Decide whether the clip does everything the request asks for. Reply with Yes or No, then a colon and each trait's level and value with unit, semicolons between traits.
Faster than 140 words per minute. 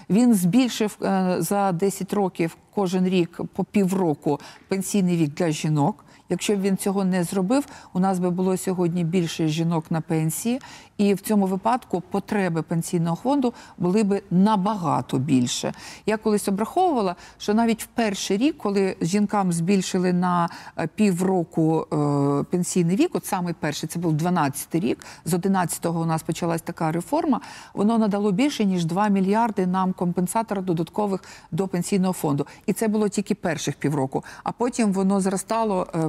Yes: average, 150 wpm